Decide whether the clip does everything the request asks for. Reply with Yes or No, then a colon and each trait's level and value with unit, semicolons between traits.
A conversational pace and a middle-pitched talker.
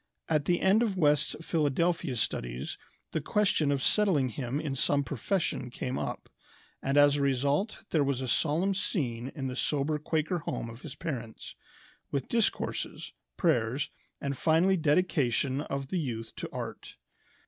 Yes: average, 155 wpm; medium, 145 Hz